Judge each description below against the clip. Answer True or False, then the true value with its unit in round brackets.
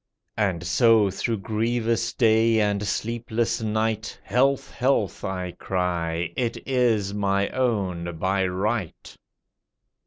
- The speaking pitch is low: True (105 Hz)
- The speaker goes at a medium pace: False (105 wpm)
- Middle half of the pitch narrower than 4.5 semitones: True (3.5 semitones)